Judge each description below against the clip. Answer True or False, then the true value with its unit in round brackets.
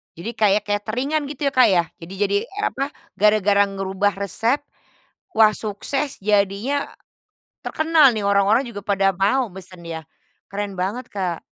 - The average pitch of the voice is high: True (205 Hz)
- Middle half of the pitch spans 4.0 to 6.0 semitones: True (4.3 semitones)